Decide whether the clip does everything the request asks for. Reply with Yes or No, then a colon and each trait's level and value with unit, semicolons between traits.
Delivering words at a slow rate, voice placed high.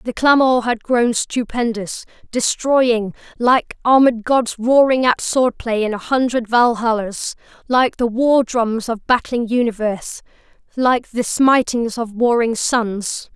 Yes: slow, 130 wpm; high, 240 Hz